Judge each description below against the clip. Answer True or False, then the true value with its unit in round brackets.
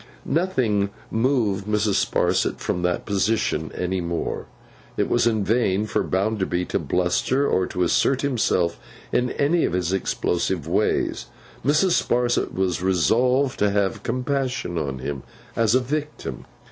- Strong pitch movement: True (5.8 semitones)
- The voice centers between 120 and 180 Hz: False (105 Hz)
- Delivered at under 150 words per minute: True (140 wpm)